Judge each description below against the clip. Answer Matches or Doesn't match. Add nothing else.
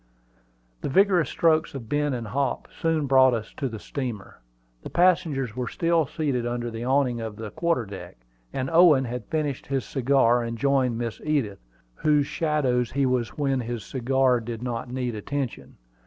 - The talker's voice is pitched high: Doesn't match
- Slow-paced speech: Doesn't match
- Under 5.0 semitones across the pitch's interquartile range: Matches